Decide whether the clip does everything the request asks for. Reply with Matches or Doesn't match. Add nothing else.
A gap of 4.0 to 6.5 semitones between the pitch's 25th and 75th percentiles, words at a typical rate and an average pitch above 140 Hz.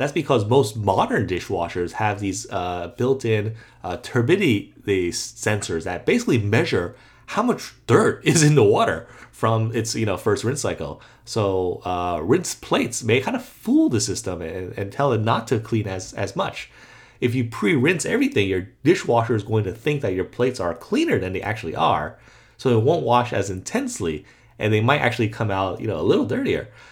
Doesn't match